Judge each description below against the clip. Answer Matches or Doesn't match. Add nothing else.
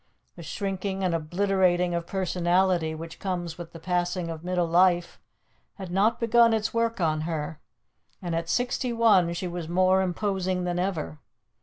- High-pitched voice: Doesn't match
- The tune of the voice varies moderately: Doesn't match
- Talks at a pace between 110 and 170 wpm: Matches